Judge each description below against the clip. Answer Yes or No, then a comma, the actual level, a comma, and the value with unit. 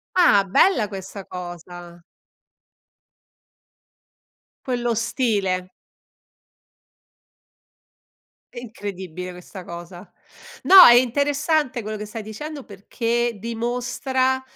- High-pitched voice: Yes, high, 220 Hz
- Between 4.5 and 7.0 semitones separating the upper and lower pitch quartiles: Yes, average, 5.1 semitones